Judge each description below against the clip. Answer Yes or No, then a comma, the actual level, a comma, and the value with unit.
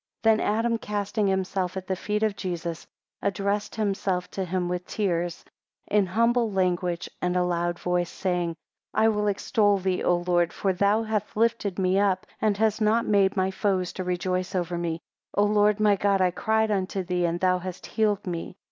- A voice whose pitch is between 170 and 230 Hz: Yes, high, 190 Hz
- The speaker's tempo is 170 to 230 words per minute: Yes, average, 190 wpm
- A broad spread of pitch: No, average, 2.7 semitones